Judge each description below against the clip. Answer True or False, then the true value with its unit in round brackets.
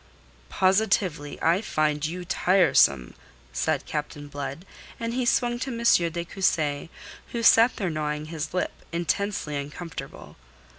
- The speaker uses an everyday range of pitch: True (5.0 semitones)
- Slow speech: True (130 wpm)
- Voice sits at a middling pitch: True (170 Hz)